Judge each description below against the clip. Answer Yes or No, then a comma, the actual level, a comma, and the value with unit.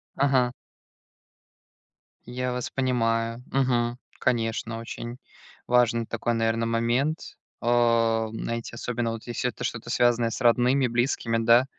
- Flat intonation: Yes, narrow, 1.4 semitones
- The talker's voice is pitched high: No, low, 120 Hz